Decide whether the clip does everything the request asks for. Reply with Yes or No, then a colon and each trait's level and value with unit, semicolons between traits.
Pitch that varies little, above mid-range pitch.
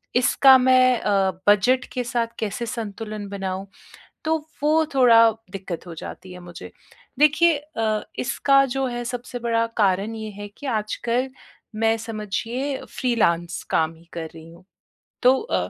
No: average, 4.4 semitones; high, 230 Hz